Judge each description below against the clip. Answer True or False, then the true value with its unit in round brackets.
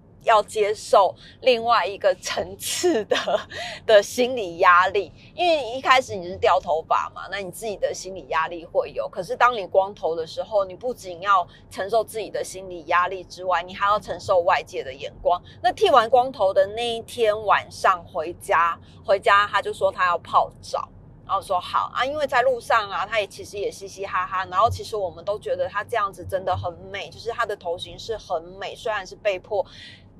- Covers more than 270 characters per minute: True (285 characters per minute)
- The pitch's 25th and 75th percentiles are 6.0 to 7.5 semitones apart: False (5.2 semitones)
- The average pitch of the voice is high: True (205 Hz)